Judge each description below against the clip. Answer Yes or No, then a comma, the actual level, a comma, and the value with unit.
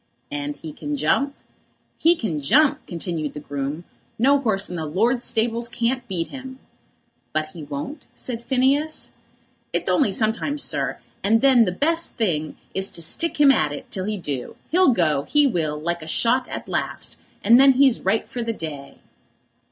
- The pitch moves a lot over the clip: Yes, wide, 8.9 semitones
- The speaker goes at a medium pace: Yes, average, 175 wpm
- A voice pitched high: Yes, high, 220 Hz